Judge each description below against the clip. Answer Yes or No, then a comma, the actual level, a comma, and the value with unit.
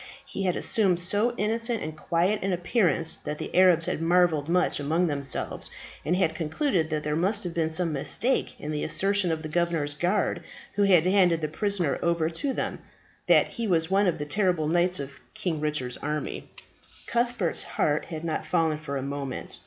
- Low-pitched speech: No, medium, 170 Hz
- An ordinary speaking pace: Yes, average, 190 wpm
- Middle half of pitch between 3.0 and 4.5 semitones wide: Yes, average, 3.7 semitones